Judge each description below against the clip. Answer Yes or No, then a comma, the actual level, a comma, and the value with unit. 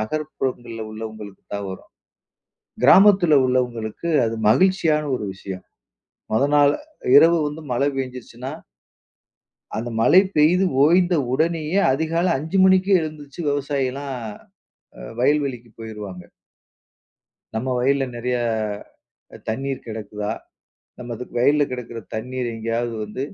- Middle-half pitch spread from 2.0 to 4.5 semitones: No, average, 5.1 semitones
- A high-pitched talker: No, low, 130 Hz